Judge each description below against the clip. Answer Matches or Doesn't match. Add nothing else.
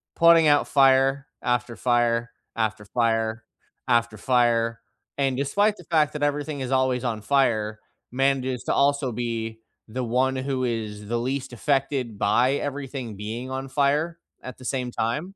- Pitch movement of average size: Matches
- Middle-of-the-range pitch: Doesn't match